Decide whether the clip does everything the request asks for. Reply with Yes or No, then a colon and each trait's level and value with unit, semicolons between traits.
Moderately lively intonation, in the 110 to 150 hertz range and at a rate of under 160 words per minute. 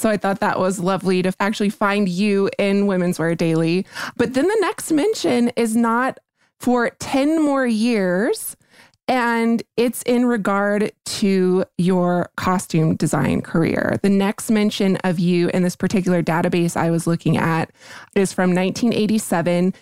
No: average, 4.2 semitones; high, 200 Hz; average, 150 wpm